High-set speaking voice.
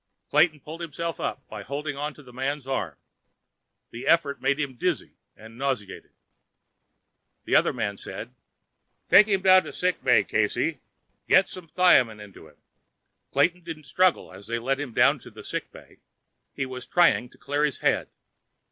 No: medium, 140 Hz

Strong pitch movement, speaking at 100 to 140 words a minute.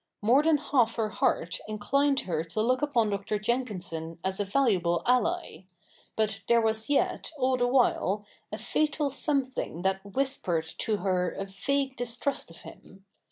No: wide, 5.7 semitones; average, 160 wpm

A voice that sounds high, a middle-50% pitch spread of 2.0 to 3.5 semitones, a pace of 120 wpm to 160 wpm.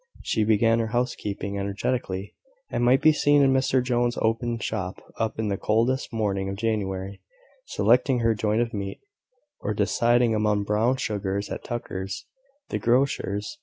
No: low, 110 Hz; average, 3.2 semitones; average, 150 wpm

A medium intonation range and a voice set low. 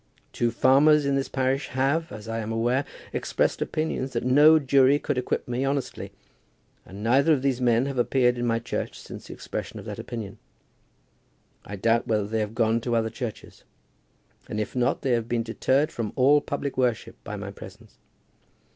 Yes: average, 3.1 semitones; low, 125 Hz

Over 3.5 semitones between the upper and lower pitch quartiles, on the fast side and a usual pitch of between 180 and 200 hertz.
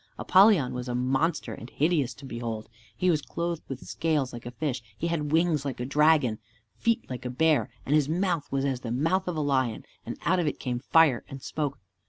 No: average, 4.5 semitones; fast, 220 wpm; medium, 145 Hz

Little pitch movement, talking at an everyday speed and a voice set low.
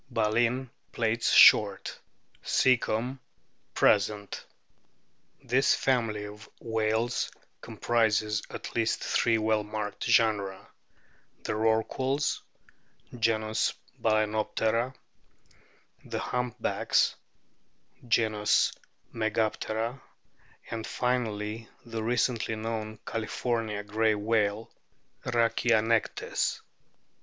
No: narrow, 1.5 semitones; slow, 75 wpm; low, 110 Hz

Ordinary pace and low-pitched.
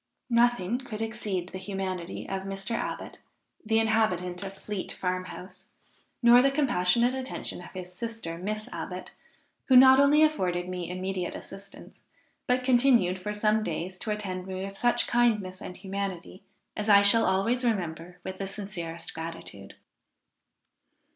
No: average, 145 wpm; high, 195 Hz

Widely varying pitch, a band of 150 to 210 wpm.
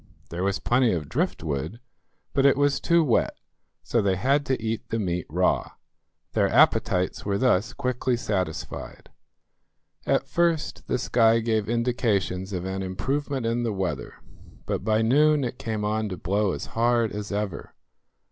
No: average, 4.7 semitones; average, 155 wpm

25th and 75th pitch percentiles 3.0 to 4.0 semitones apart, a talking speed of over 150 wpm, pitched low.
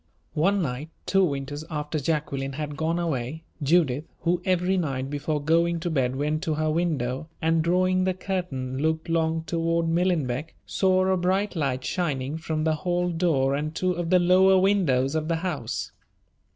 No: average, 3.6 semitones; average, 170 wpm; medium, 160 Hz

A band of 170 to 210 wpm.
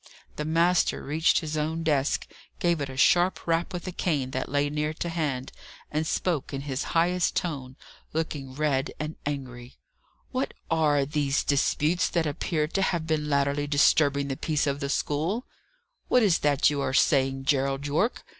Yes: average, 175 wpm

